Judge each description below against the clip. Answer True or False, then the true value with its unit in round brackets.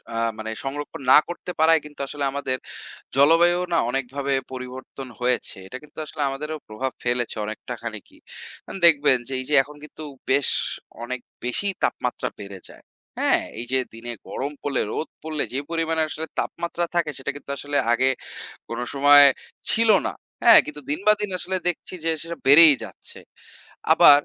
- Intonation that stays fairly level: False (3.8 semitones)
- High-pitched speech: False (145 Hz)